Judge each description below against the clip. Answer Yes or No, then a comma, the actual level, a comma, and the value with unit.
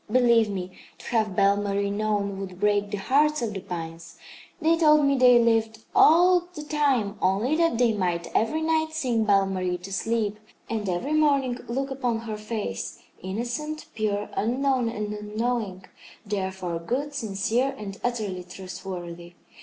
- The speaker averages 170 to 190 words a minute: No, average, 155 wpm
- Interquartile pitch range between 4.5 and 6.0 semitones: Yes, average, 4.9 semitones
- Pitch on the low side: No, high, 215 Hz